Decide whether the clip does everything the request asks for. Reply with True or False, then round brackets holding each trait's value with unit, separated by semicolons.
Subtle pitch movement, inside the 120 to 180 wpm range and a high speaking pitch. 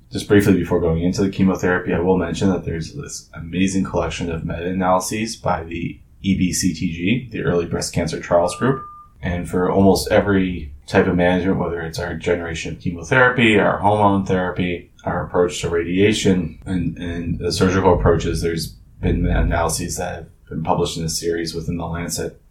False (2.2 semitones; 170 wpm; 90 Hz)